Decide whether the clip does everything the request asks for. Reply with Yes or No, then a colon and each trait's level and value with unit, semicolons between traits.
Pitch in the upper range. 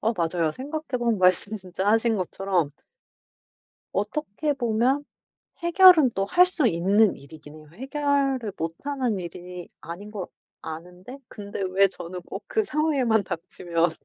Yes: high, 205 Hz